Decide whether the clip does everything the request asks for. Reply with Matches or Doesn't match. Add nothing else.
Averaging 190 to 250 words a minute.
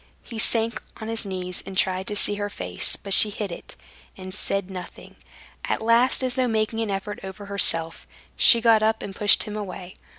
Matches